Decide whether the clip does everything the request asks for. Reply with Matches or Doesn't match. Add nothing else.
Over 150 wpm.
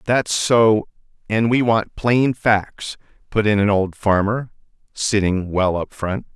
Doesn't match